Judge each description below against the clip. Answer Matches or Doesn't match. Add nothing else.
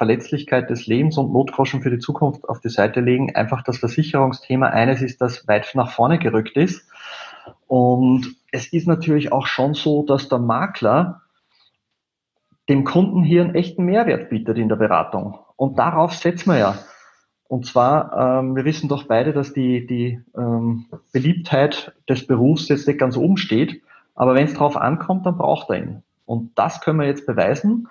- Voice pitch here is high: Doesn't match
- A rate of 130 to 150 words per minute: Doesn't match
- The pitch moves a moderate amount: Matches